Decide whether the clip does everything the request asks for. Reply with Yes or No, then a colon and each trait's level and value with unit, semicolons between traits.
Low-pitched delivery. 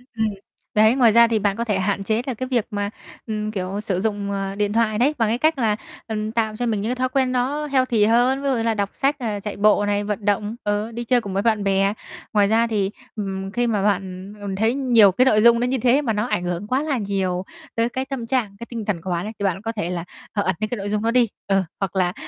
No: high, 215 Hz